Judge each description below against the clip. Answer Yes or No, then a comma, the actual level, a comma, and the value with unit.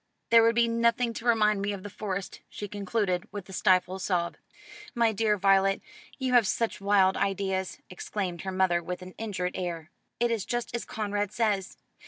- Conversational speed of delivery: Yes, average, 185 wpm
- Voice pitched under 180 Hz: No, high, 200 Hz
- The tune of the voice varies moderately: Yes, average, 3.2 semitones